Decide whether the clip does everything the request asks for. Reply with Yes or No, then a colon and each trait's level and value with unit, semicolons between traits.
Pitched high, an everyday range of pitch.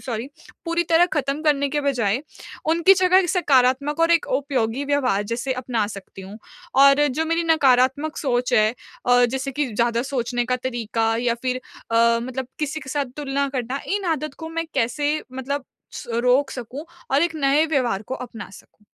Yes: very high, 270 Hz; average, 3.6 semitones